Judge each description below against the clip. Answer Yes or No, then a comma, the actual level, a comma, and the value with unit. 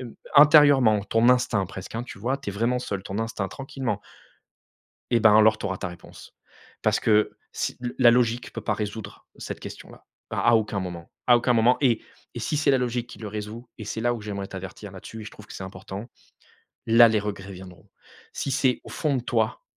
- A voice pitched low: Yes, low, 110 Hz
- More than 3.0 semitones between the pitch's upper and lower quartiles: Yes, average, 3.4 semitones